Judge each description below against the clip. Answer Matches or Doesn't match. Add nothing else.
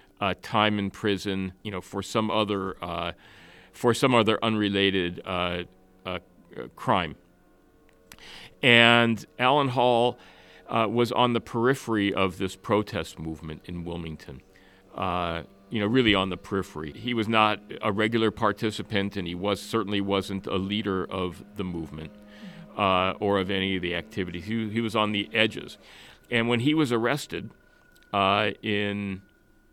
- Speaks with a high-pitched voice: Doesn't match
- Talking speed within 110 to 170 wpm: Matches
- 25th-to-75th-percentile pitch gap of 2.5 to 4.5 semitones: Matches